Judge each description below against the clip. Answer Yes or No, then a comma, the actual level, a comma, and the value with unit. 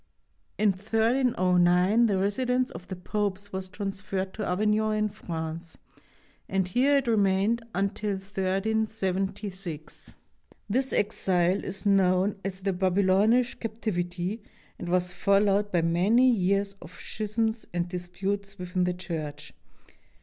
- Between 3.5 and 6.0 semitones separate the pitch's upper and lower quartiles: No, average, 2.9 semitones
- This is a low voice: No, high, 195 Hz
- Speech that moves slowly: Yes, slow, 120 wpm